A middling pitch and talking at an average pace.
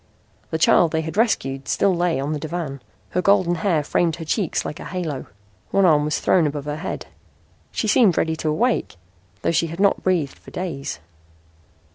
Yes: medium, 165 Hz; average, 190 wpm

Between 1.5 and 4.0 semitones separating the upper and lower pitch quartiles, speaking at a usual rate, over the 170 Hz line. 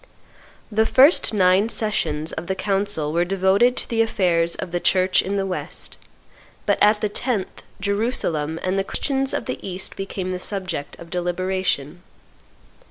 Yes: average, 2.8 semitones; average, 160 wpm; high, 190 Hz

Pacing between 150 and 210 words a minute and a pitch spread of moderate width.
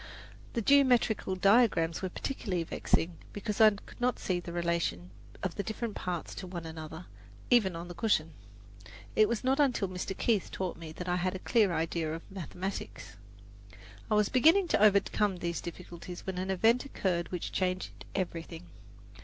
Yes: average, 170 wpm; average, 4.0 semitones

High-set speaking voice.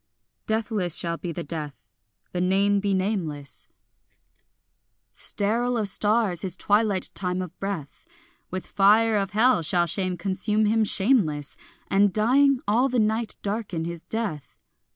Yes: high, 200 Hz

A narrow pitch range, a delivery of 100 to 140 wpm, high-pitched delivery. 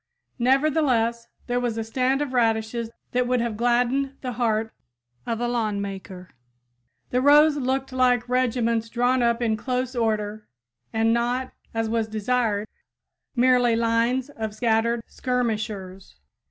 Yes: narrow, 2.1 semitones; slow, 135 wpm; high, 235 Hz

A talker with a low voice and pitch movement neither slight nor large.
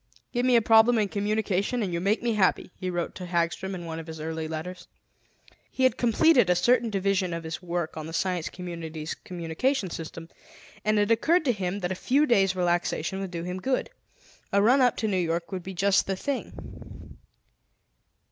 No: medium, 185 Hz; average, 4.4 semitones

